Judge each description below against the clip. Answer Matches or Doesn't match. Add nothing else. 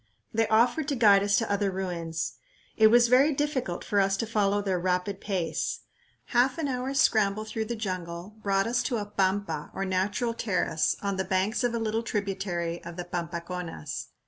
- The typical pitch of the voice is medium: Doesn't match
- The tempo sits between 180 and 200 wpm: Matches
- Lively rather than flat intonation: Doesn't match